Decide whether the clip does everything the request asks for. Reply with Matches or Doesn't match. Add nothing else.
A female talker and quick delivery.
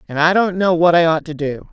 Matches